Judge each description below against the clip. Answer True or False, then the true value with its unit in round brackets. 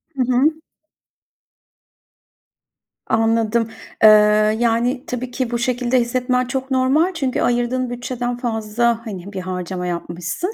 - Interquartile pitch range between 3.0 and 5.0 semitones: False (2.4 semitones)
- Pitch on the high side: True (240 Hz)